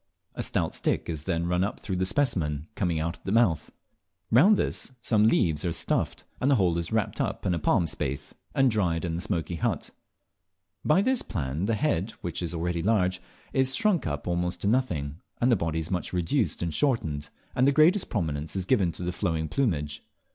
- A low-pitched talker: Yes, very low, 90 Hz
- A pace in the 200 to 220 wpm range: Yes, fast, 205 wpm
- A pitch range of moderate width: No, wide, 5.8 semitones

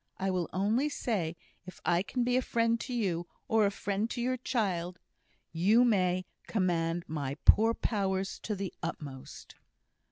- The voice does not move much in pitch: No, average, 4.7 semitones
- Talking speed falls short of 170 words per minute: Yes, average, 160 wpm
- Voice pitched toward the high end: Yes, high, 195 Hz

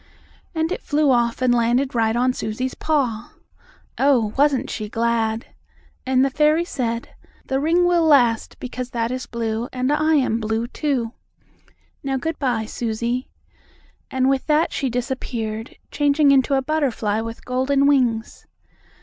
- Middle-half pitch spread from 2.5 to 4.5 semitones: Yes, average, 3.5 semitones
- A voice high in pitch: Yes, very high, 255 Hz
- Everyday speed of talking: Yes, average, 150 wpm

